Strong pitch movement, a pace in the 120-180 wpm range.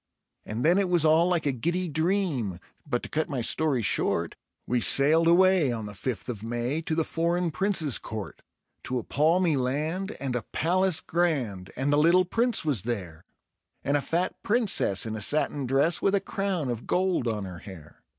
No: wide, 6.6 semitones; average, 190 wpm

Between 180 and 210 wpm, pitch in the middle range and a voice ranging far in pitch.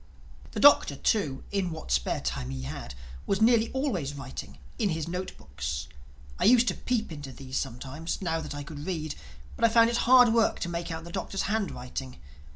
Yes: average, 190 wpm; medium, 165 Hz; wide, 8.4 semitones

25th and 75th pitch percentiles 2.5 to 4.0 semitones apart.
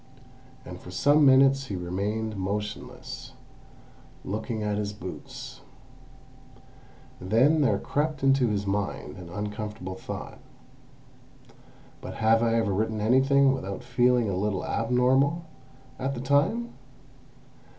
No: average, 4.8 semitones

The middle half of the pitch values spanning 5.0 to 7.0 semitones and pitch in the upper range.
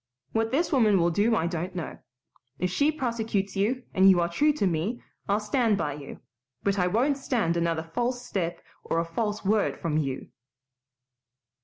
Yes: wide, 5.6 semitones; high, 200 Hz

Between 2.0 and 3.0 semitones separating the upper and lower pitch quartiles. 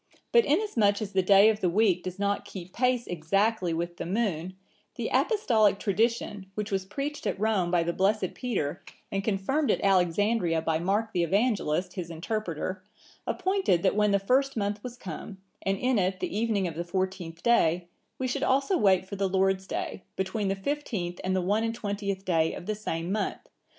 No: average, 3.5 semitones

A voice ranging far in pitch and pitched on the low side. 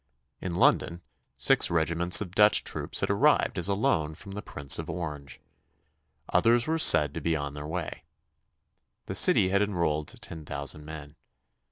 No: average, 4.4 semitones; very low, 85 Hz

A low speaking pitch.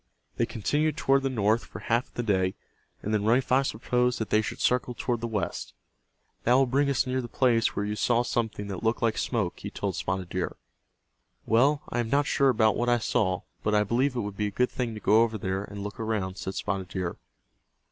Yes: low, 115 Hz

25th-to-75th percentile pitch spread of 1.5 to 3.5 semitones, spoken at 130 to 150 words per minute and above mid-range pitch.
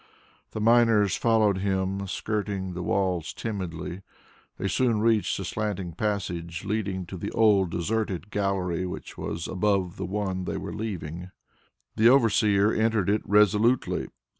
No: average, 2.7 semitones; average, 140 wpm; low, 100 Hz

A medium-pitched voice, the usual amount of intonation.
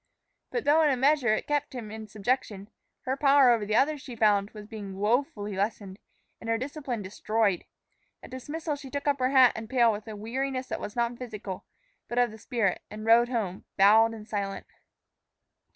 No: high, 230 Hz; average, 3.9 semitones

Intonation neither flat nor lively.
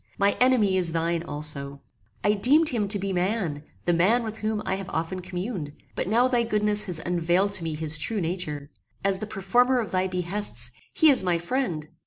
Yes: average, 4.3 semitones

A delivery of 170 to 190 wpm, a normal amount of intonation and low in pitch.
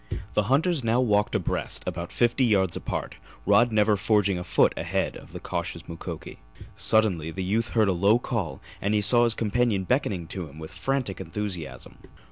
Yes: average, 180 wpm; average, 4.3 semitones; low, 105 Hz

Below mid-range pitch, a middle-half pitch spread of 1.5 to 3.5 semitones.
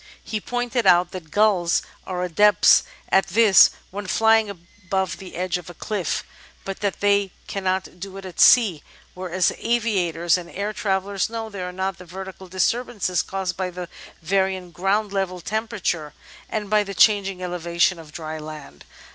No: high, 190 Hz; narrow, 2.4 semitones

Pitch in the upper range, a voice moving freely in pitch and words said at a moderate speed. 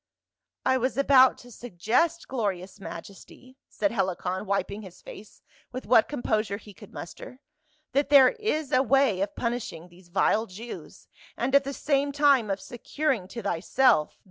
Yes: high, 240 Hz; wide, 5.7 semitones; average, 170 wpm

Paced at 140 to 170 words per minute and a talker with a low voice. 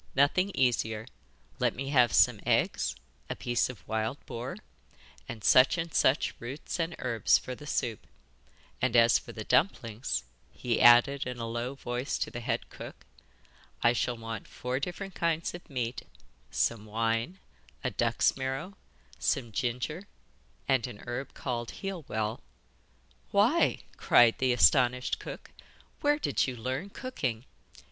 Yes: average, 145 wpm; low, 125 Hz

